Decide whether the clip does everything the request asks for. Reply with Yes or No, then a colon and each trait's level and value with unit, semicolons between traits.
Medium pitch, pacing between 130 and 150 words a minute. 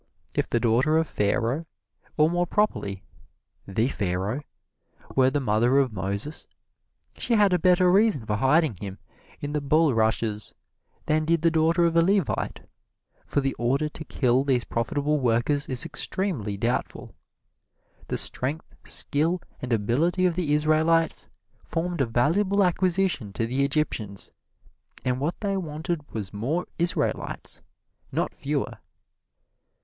Yes: medium, 145 Hz; slow, 135 wpm